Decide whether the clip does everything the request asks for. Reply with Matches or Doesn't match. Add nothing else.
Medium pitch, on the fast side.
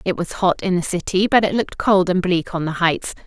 Matches